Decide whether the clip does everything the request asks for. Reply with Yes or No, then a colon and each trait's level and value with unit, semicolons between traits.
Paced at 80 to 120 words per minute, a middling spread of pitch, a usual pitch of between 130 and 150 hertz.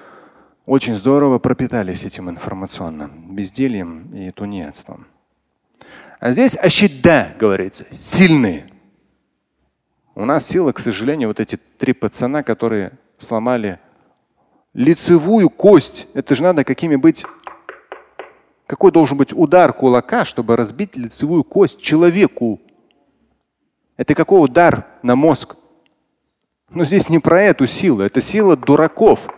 No: slow, 110 wpm; wide, 7.3 semitones; low, 135 Hz